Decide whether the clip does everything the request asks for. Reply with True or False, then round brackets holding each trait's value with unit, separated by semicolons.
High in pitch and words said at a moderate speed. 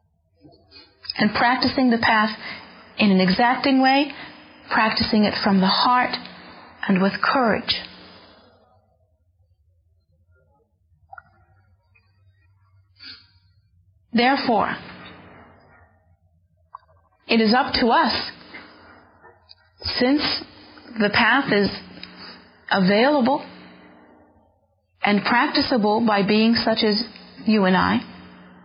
False (195 Hz; 75 wpm)